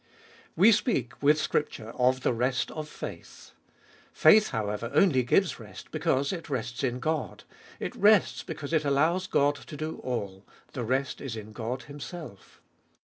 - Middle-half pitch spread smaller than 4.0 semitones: No, average, 4.5 semitones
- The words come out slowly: No, average, 155 wpm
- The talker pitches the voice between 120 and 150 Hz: Yes, medium, 140 Hz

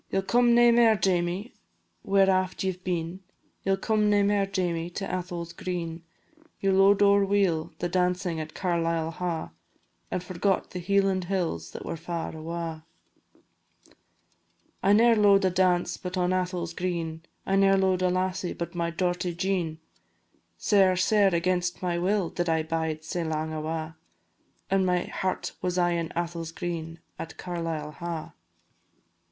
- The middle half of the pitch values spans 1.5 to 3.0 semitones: Yes, narrow, 2.4 semitones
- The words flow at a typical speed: Yes, average, 160 wpm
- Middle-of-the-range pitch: Yes, medium, 180 Hz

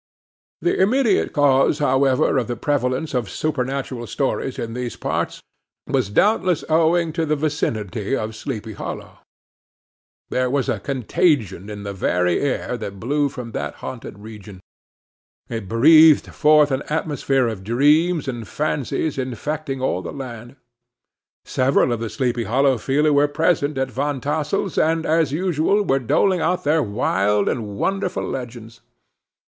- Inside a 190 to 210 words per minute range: No, average, 145 wpm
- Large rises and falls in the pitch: No, average, 4.8 semitones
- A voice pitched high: No, low, 135 Hz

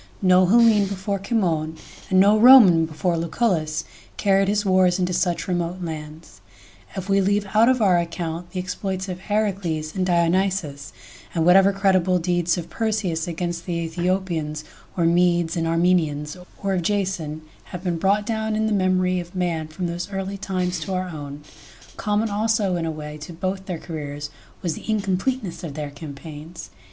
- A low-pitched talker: No, medium, 180 Hz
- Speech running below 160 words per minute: No, average, 170 wpm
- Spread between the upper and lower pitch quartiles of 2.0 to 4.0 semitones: Yes, average, 3.1 semitones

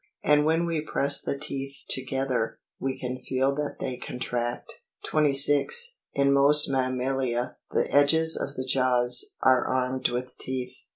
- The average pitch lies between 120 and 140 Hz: Yes, low, 135 Hz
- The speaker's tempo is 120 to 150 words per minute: Yes, average, 140 wpm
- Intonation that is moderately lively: No, narrow, 2.1 semitones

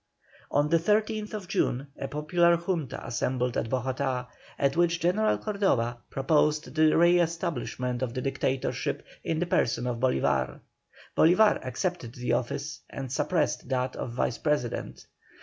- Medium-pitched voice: Yes, medium, 145 Hz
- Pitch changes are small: No, average, 5.3 semitones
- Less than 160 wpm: Yes, average, 140 wpm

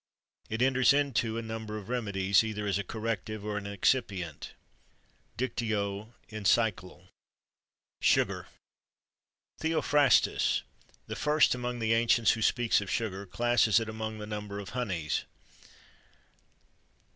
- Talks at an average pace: No, slow, 120 wpm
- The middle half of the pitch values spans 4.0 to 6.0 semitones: No, average, 2.9 semitones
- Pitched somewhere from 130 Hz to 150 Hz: No, low, 110 Hz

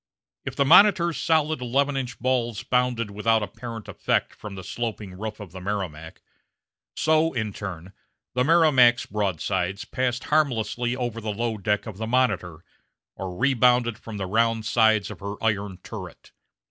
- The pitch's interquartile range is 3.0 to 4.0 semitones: Yes, average, 3.7 semitones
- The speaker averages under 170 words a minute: Yes, average, 155 wpm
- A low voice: Yes, low, 115 Hz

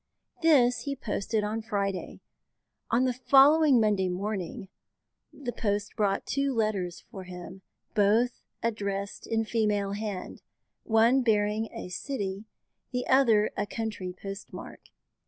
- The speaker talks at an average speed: No, slow, 125 wpm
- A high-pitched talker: Yes, high, 215 Hz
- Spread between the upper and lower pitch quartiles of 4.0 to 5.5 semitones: No, average, 3.4 semitones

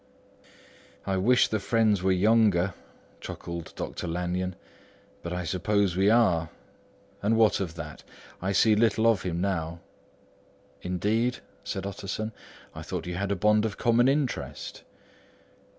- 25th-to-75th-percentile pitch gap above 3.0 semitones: Yes, average, 3.6 semitones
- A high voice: No, low, 100 Hz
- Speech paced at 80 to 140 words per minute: Yes, slow, 135 wpm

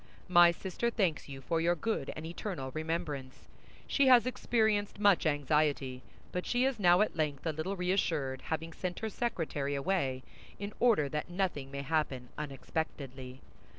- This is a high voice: No, medium, 160 Hz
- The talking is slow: No, average, 155 wpm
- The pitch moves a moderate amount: No, wide, 5.7 semitones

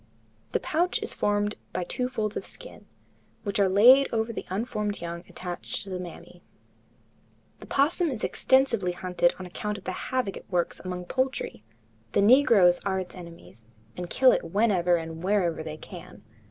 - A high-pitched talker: Yes, high, 195 Hz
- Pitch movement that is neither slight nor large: Yes, average, 4.5 semitones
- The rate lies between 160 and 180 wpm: Yes, average, 170 wpm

